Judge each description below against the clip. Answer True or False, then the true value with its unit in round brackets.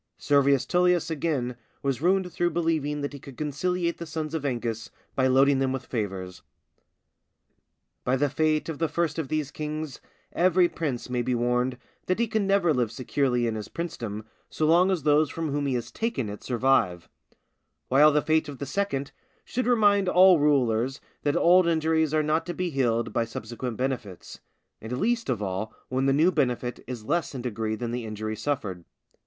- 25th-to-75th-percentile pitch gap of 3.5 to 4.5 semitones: False (5.1 semitones)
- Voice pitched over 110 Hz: True (140 Hz)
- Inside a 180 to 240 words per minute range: True (185 wpm)